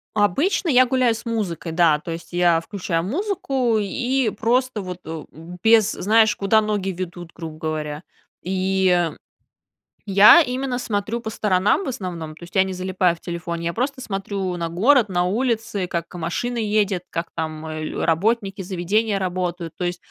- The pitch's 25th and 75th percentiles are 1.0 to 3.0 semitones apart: No, average, 4.6 semitones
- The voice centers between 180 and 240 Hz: Yes, high, 190 Hz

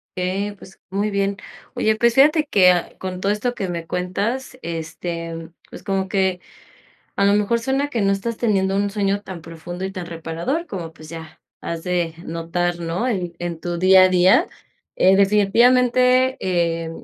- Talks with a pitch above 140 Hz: Yes, high, 190 Hz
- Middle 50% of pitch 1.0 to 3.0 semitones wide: No, average, 3.4 semitones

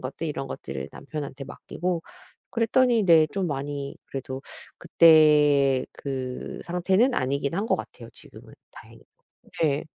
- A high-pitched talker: No, medium, 150 Hz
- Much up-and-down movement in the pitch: No, average, 4.2 semitones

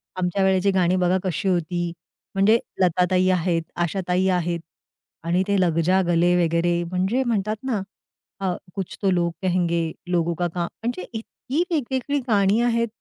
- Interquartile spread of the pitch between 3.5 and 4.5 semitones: No, narrow, 2.6 semitones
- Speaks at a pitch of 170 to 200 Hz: Yes, medium, 185 Hz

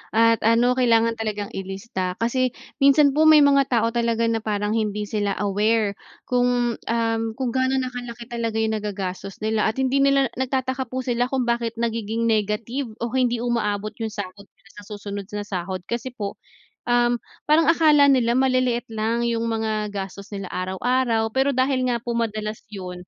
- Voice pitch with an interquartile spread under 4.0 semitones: Yes, average, 3.2 semitones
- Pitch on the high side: Yes, high, 230 Hz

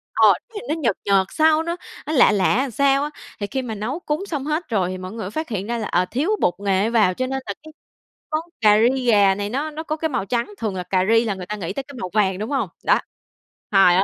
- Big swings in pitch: Yes, wide, 6.0 semitones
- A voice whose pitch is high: Yes, high, 225 Hz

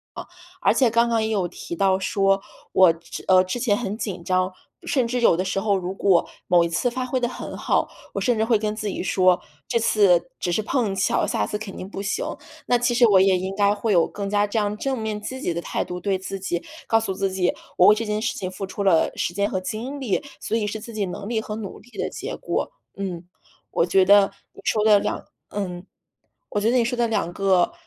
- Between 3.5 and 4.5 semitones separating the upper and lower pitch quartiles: No, average, 3.1 semitones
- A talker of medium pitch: No, high, 205 Hz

